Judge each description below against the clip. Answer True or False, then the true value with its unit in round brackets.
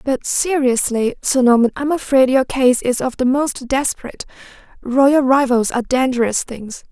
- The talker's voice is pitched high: True (260 Hz)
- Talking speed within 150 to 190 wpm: True (165 wpm)